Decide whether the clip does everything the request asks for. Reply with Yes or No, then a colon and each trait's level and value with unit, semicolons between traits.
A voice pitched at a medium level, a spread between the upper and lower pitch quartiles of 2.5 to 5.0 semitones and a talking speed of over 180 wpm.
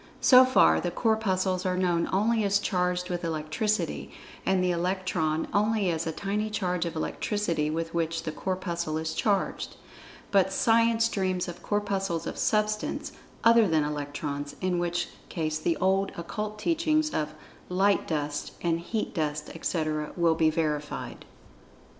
No: medium, 180 Hz; average, 4.3 semitones; average, 150 wpm